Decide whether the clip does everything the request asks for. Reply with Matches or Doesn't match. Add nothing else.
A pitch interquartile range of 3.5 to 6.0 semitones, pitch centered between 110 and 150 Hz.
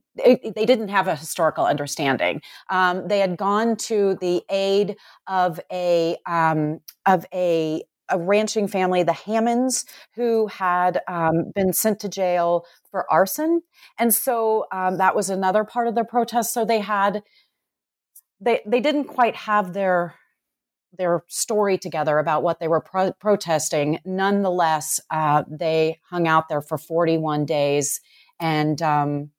Doesn't match